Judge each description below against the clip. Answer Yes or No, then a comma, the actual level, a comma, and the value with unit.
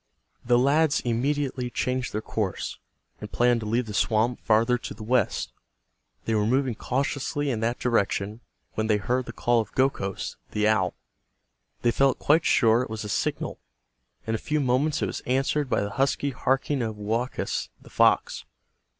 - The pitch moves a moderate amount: Yes, average, 3.4 semitones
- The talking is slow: No, average, 175 wpm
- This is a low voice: Yes, low, 120 Hz